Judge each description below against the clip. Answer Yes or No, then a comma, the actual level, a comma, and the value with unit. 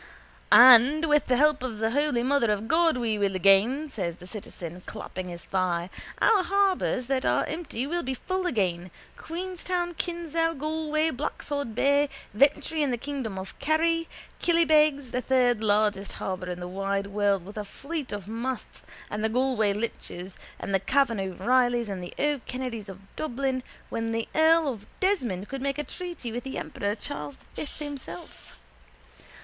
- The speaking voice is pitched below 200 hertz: No, very high, 250 Hz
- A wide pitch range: Yes, wide, 6.9 semitones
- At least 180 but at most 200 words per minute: No, average, 165 wpm